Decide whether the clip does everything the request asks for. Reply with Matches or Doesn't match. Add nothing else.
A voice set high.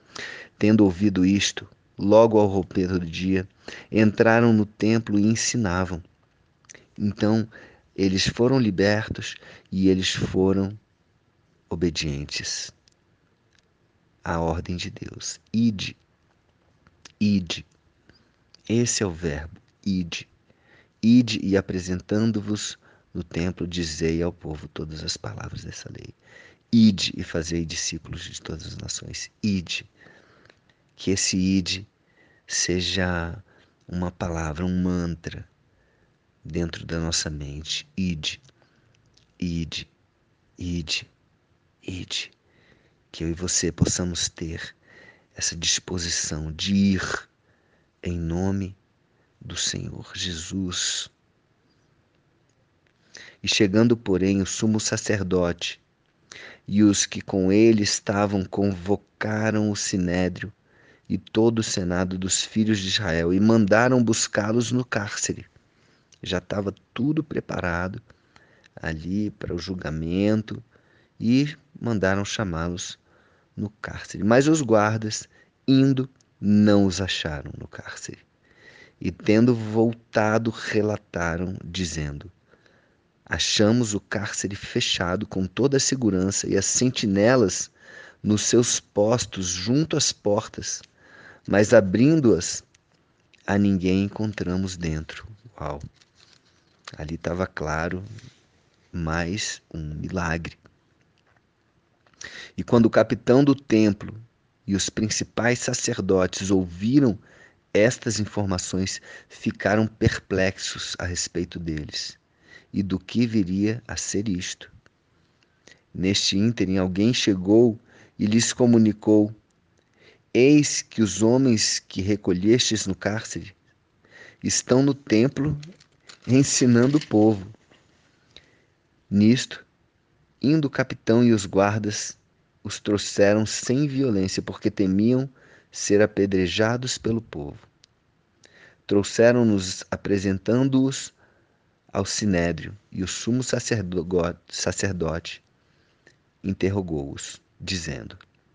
Doesn't match